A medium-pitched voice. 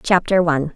Yes: medium, 170 Hz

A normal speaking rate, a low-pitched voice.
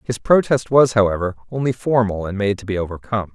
Yes: average, 195 wpm; low, 110 Hz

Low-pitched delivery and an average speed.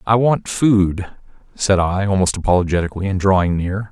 Yes: very low, 95 Hz; average, 155 wpm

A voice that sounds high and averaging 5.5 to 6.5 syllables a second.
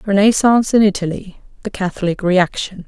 Yes: high, 195 Hz; 5.6 syllables/s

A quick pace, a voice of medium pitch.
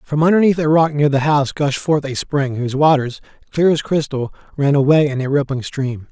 Yes: fast, 215 wpm; medium, 145 Hz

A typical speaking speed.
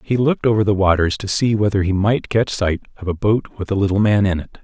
No: fast, 270 wpm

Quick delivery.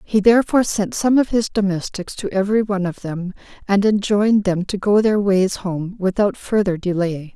No: average, 190 wpm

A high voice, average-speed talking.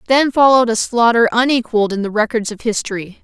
Yes: high, 230 Hz; average, 185 wpm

